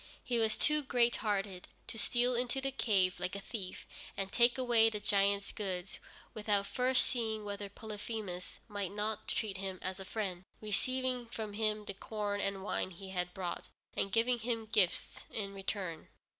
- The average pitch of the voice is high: Yes, high, 210 Hz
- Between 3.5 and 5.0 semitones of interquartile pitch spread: No, average, 2.8 semitones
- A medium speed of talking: Yes, average, 170 wpm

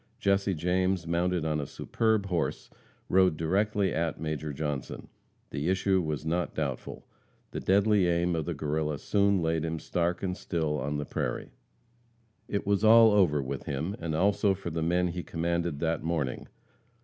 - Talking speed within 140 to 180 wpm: Yes, average, 165 wpm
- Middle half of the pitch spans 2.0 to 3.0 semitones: No, average, 3.5 semitones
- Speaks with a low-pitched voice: Yes, very low, 85 Hz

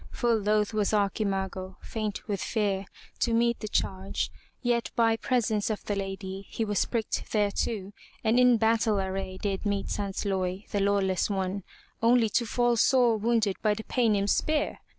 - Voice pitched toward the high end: Yes, high, 210 Hz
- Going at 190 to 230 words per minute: No, average, 160 wpm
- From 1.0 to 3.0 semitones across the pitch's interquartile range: Yes, average, 2.7 semitones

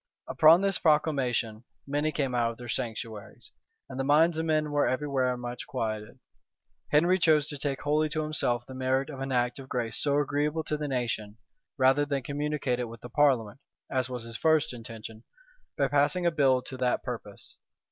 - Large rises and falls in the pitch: No, average, 3.5 semitones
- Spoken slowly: No, average, 190 wpm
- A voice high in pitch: No, low, 135 Hz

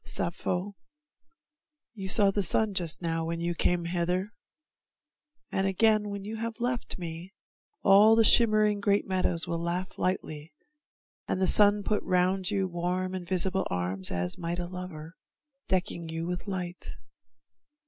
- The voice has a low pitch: No, medium, 185 Hz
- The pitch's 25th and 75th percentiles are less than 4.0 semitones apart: Yes, average, 2.9 semitones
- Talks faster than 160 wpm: No, average, 150 wpm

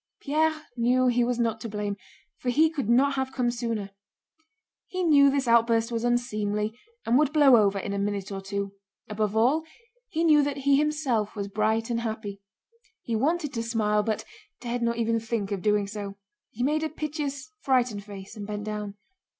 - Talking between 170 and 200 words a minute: Yes, average, 190 wpm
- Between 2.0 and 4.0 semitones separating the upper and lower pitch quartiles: No, average, 4.6 semitones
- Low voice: No, high, 230 Hz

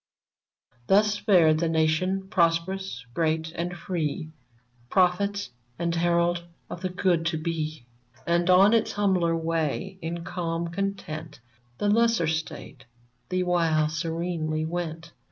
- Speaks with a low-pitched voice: No, medium, 170 Hz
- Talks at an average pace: No, slow, 120 wpm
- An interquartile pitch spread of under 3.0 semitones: Yes, narrow, 2.5 semitones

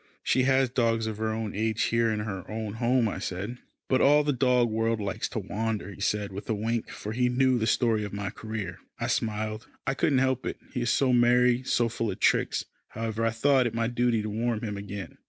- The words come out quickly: Yes, fast, 230 wpm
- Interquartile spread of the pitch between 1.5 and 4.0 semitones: Yes, narrow, 2.5 semitones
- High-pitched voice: No, low, 115 Hz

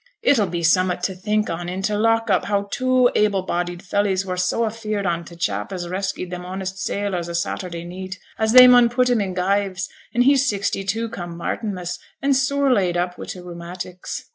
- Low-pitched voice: No, high, 190 Hz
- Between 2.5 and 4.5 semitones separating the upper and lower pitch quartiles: Yes, average, 3.5 semitones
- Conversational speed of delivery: No, fast, 210 wpm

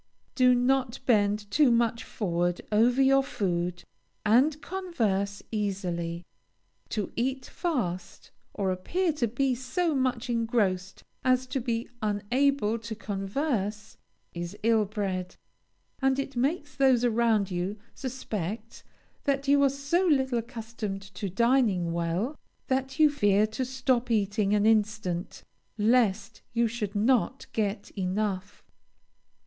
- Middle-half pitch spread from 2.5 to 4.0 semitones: No, average, 4.6 semitones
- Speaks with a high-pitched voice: Yes, high, 230 Hz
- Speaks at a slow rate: Yes, slow, 125 wpm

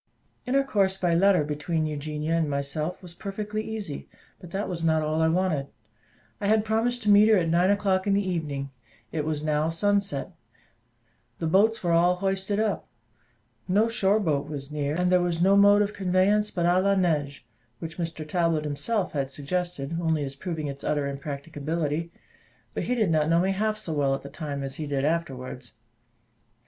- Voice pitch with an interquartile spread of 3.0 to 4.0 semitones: No, average, 4.8 semitones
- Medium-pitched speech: Yes, medium, 170 Hz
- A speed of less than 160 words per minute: No, average, 185 wpm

